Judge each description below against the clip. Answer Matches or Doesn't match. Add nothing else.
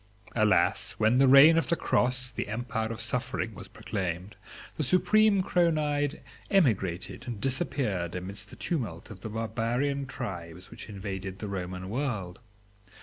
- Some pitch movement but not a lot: Doesn't match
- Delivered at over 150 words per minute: Doesn't match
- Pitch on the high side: Doesn't match